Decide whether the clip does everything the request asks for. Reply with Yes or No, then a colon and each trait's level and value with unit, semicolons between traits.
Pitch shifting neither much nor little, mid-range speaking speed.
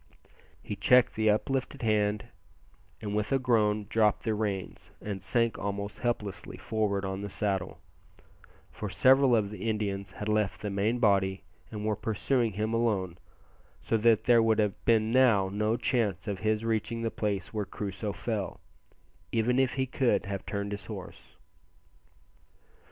No: narrow, 2.2 semitones; average, 155 wpm